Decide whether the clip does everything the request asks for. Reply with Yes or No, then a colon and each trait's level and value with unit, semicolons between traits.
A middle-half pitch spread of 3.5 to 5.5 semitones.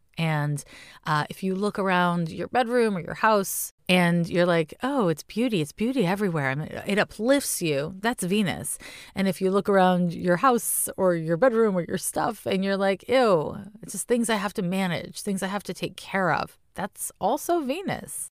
Yes: average, 3.9 semitones